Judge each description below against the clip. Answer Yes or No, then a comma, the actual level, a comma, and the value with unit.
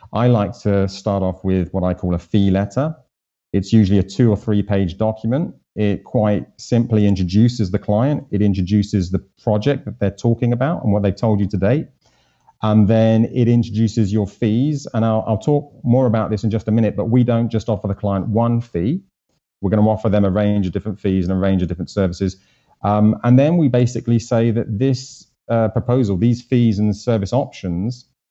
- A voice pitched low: Yes, low, 110 Hz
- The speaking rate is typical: No, fast, 210 wpm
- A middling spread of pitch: Yes, average, 3.1 semitones